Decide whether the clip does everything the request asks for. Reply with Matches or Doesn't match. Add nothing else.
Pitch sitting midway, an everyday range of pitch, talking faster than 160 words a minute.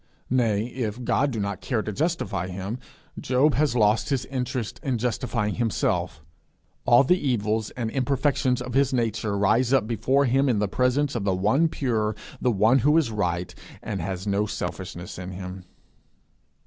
Doesn't match